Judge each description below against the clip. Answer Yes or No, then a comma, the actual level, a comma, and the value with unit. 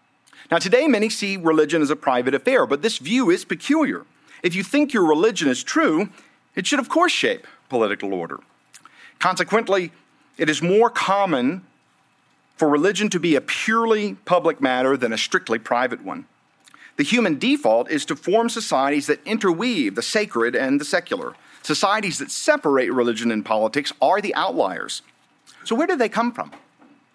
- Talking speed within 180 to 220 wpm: No, average, 165 wpm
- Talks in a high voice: Yes, high, 215 Hz